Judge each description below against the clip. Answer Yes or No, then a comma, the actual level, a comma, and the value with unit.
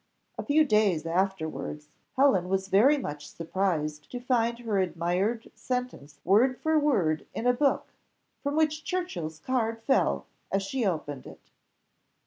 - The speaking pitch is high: Yes, high, 200 Hz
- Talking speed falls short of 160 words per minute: Yes, average, 140 wpm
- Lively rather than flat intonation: Yes, wide, 7.5 semitones